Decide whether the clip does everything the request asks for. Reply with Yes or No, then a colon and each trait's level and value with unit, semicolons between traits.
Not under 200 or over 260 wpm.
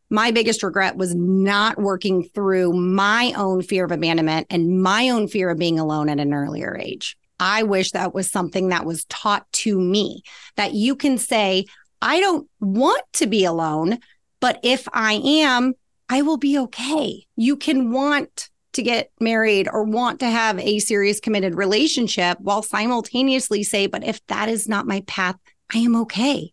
No: average, 175 wpm